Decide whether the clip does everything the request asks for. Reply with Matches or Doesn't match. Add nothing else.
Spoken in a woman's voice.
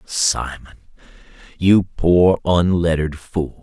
Doesn't match